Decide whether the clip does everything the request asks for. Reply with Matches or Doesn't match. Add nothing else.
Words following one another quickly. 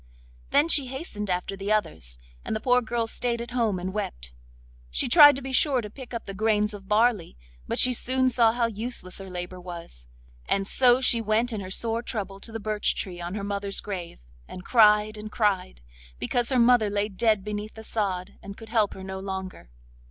Matches